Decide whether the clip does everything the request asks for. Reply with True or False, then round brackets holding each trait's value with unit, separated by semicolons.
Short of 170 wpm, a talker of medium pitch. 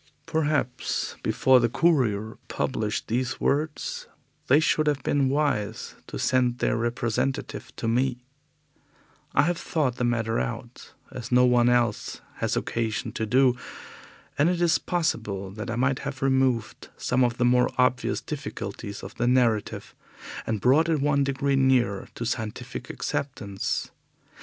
False (145 wpm; 125 Hz)